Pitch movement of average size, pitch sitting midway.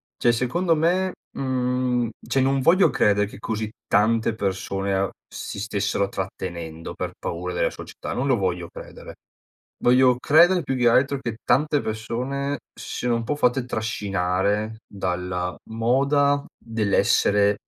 No: average, 5.0 semitones; low, 115 Hz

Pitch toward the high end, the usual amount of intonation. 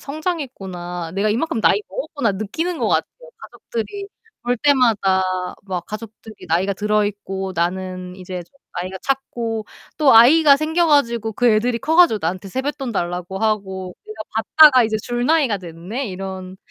No: high, 215 Hz; wide, 6.3 semitones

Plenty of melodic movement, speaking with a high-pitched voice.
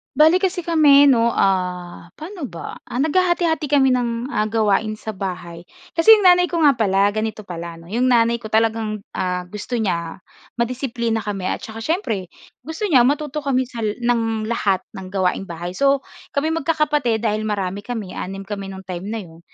Yes: wide, 6.3 semitones; high, 225 Hz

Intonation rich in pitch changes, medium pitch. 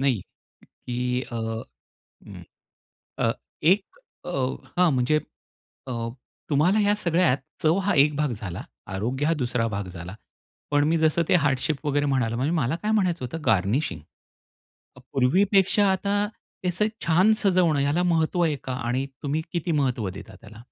Yes: wide, 6.1 semitones; medium, 145 Hz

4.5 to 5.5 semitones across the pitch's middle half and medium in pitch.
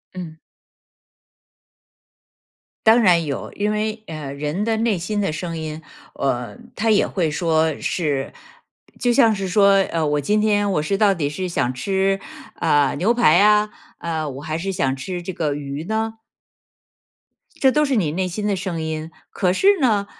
Yes: average, 5.2 semitones; medium, 180 Hz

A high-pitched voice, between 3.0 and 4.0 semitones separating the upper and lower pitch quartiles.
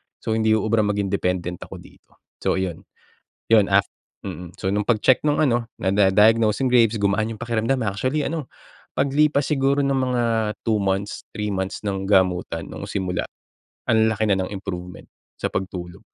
No: low, 105 Hz; average, 3.7 semitones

